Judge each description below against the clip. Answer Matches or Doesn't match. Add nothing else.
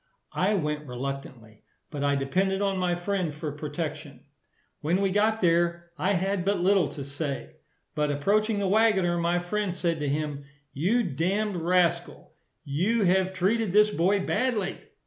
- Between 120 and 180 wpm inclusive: Matches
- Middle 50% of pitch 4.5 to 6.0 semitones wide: Matches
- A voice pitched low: Doesn't match